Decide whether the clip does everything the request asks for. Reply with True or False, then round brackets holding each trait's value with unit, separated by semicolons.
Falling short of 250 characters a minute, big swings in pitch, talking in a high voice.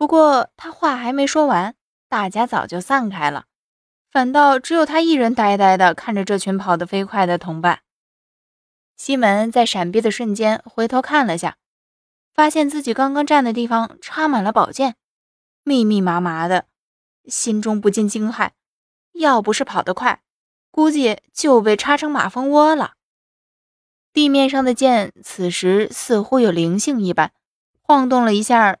True (230 characters per minute; 5.8 semitones; 235 Hz)